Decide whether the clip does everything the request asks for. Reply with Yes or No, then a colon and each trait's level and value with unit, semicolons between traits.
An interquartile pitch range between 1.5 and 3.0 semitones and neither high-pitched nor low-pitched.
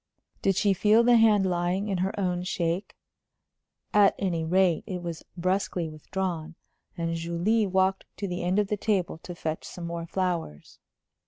Yes: narrow, 2.5 semitones; medium, 180 Hz